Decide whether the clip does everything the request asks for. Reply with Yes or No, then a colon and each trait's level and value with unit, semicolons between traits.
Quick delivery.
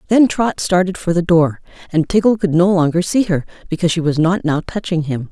Yes: fast, 225 wpm